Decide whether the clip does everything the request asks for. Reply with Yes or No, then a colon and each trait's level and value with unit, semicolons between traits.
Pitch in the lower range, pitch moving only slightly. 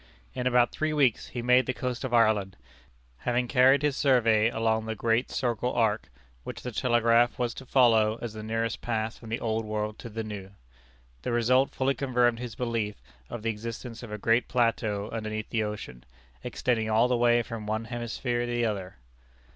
Yes: low, 115 Hz; narrow, 2.1 semitones